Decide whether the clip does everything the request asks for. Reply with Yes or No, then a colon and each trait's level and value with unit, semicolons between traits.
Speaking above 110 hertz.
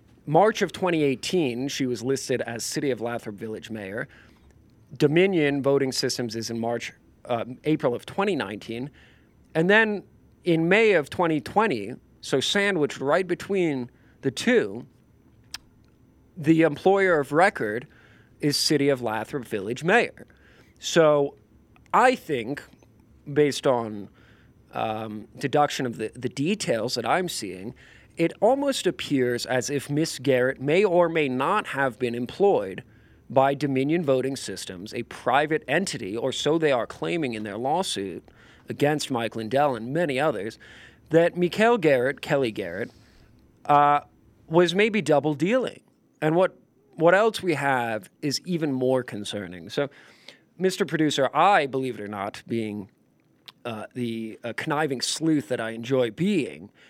Yes: medium, 140 Hz